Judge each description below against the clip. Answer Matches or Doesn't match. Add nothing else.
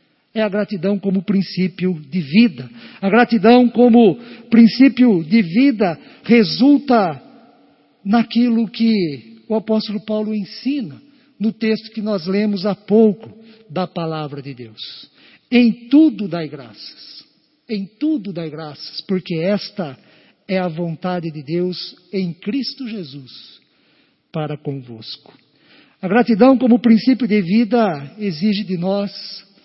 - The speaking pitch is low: Doesn't match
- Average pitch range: Matches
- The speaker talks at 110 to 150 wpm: Matches